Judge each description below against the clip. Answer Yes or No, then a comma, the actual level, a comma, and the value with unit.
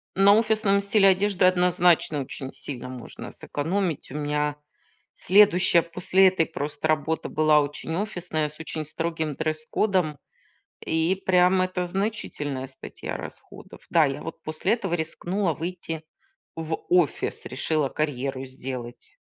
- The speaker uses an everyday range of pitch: Yes, average, 3.7 semitones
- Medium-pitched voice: Yes, medium, 165 Hz